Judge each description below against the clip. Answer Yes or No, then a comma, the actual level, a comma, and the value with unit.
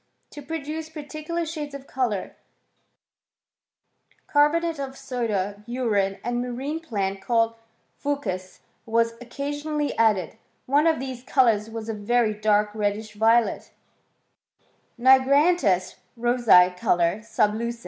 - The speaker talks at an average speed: No, slow, 120 wpm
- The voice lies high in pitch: Yes, high, 240 Hz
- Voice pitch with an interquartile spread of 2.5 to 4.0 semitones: No, average, 5.2 semitones